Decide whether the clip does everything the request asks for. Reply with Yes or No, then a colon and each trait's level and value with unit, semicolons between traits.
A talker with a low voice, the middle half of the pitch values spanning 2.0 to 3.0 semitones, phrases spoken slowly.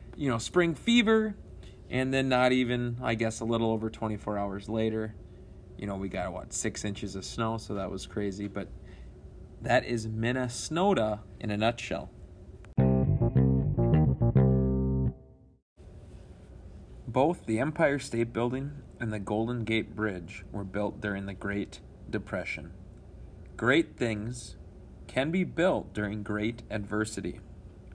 No: low, 105 Hz; average, 4.0 semitones; slow, 130 wpm